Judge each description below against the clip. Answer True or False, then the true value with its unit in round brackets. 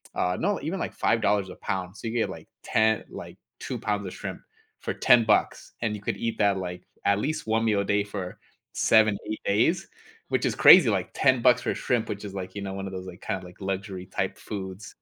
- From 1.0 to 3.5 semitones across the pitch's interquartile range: True (2.9 semitones)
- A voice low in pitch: True (100 Hz)